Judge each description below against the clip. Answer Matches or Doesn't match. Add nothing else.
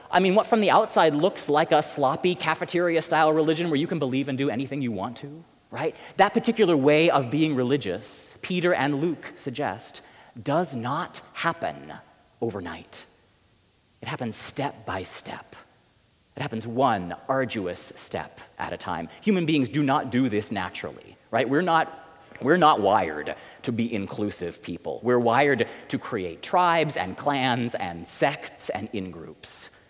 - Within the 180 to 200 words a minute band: Doesn't match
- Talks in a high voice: Doesn't match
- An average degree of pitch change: Doesn't match